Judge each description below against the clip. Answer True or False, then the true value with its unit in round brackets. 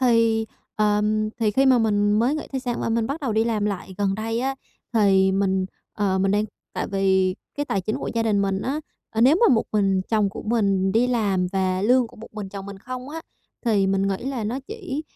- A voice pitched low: False (215 Hz)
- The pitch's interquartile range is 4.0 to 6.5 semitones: False (3.5 semitones)